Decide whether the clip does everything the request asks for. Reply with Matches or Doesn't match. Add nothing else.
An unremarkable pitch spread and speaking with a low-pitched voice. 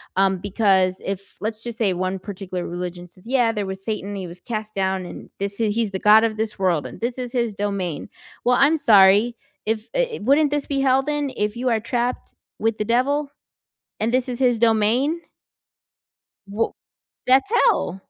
Doesn't match